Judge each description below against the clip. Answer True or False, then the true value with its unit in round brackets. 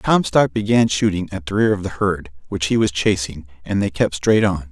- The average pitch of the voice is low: True (95 Hz)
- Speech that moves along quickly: True (230 wpm)